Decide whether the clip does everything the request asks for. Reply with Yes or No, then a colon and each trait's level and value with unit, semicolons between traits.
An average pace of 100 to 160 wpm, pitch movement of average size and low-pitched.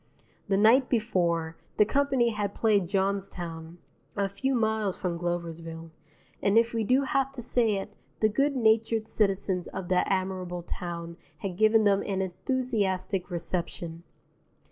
No: average, 145 wpm; average, 4.0 semitones; high, 195 Hz